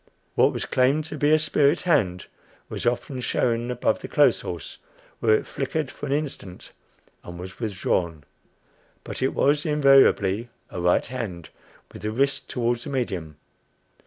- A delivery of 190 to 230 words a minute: No, average, 160 wpm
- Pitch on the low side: Yes, low, 125 Hz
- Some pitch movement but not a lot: No, wide, 6.8 semitones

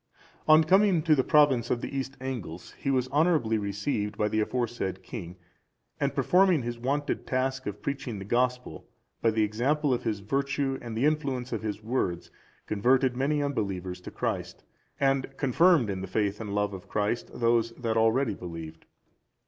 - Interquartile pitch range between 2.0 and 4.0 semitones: No, average, 4.8 semitones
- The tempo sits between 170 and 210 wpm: Yes, average, 175 wpm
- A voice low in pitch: Yes, low, 120 Hz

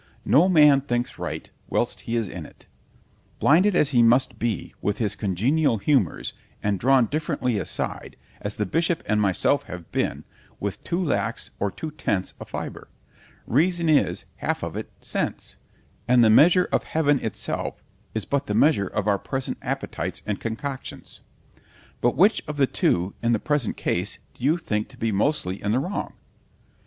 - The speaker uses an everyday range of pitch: No, wide, 6.2 semitones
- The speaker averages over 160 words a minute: Yes, average, 170 wpm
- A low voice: Yes, low, 120 Hz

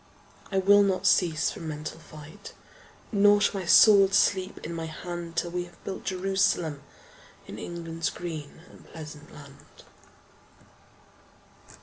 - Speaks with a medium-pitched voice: Yes, medium, 175 Hz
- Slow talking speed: Yes, slow, 130 wpm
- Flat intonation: No, average, 3.5 semitones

